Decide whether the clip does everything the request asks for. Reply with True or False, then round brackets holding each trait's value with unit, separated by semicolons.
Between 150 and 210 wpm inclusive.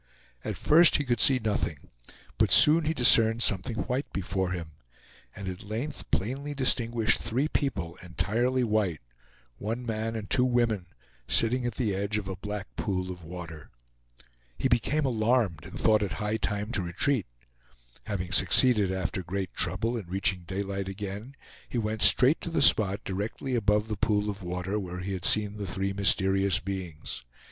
True (170 wpm)